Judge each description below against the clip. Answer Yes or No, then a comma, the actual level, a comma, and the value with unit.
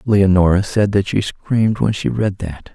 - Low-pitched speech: Yes, low, 100 Hz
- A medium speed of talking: Yes, average, 195 wpm